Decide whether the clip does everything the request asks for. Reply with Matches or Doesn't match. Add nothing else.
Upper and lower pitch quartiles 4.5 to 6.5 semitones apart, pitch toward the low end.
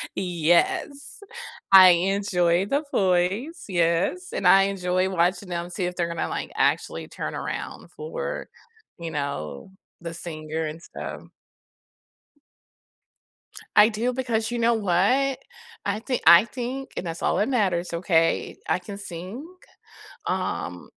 Doesn't match